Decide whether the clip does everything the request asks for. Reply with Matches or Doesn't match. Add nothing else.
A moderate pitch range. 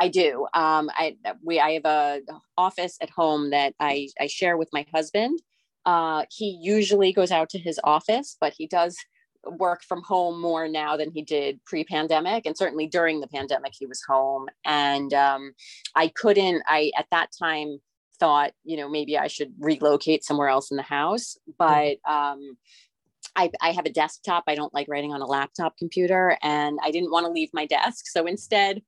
Matches